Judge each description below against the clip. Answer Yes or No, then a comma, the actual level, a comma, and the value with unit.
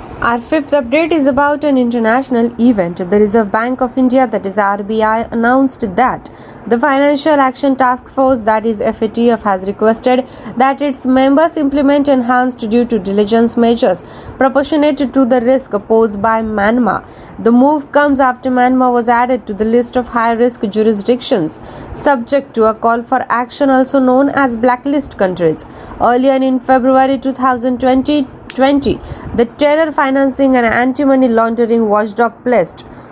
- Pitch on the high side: Yes, very high, 250 Hz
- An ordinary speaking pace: No, fast, 145 wpm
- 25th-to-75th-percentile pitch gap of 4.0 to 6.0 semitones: No, average, 2.8 semitones